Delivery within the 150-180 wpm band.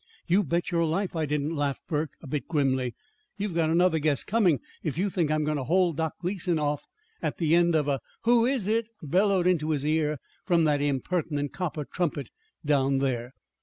No: average, 200 wpm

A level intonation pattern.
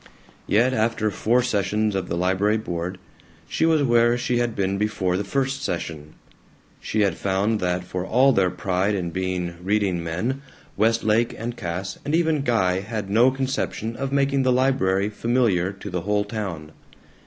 No: average, 4.6 semitones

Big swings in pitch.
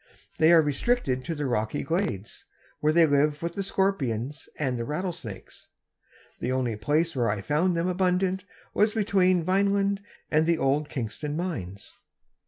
Yes: wide, 6.0 semitones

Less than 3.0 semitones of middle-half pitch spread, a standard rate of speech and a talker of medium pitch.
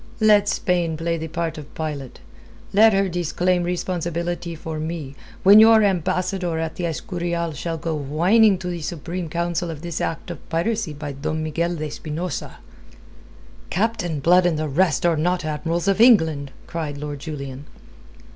Yes: narrow, 2.5 semitones; average, 160 wpm; medium, 170 Hz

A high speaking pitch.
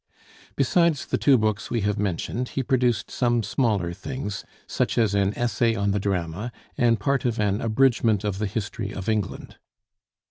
No: low, 110 Hz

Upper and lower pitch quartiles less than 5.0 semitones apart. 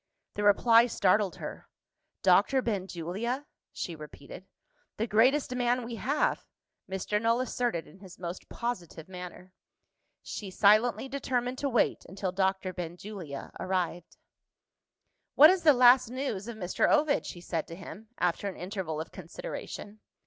No: average, 5.3 semitones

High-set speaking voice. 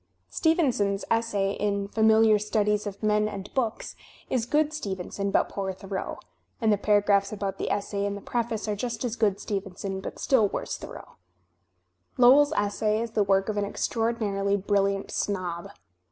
Yes: high, 205 Hz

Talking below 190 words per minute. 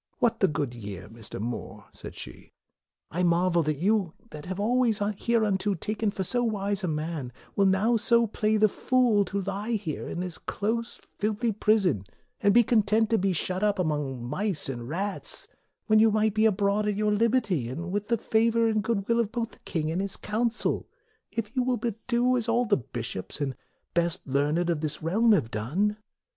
No: fast, 205 wpm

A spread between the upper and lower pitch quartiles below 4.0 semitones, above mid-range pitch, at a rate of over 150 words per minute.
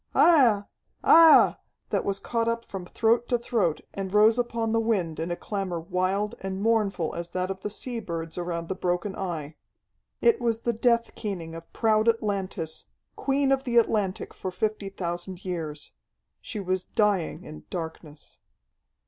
No: average, 4.6 semitones; high, 195 Hz; average, 165 wpm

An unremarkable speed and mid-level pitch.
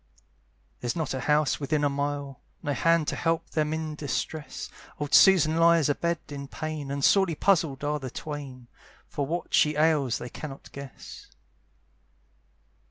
Yes: average, 160 wpm; medium, 150 Hz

